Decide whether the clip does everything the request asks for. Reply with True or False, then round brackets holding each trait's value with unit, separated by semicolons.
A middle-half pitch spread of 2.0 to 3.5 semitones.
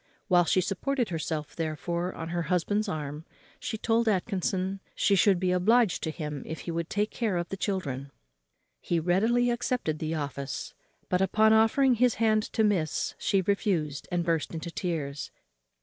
False (4.9 semitones)